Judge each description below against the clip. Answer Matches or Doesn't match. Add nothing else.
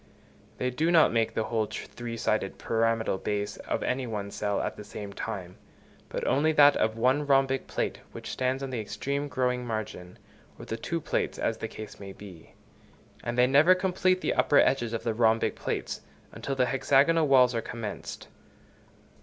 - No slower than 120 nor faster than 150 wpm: Doesn't match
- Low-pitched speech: Matches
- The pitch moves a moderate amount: Matches